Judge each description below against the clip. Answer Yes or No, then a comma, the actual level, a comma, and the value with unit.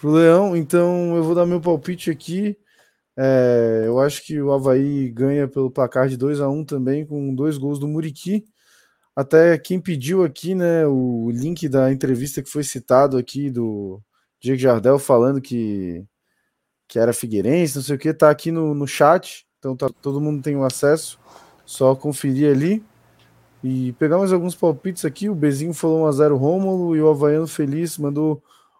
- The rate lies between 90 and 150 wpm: No, average, 175 wpm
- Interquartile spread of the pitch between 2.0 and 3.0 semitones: No, average, 3.8 semitones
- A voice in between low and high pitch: Yes, medium, 145 Hz